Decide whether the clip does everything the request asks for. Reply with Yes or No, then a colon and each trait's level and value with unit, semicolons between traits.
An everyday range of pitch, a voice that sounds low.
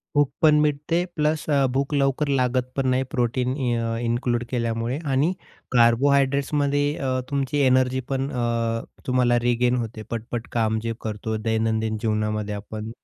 Yes: average, 3.4 semitones; low, 125 Hz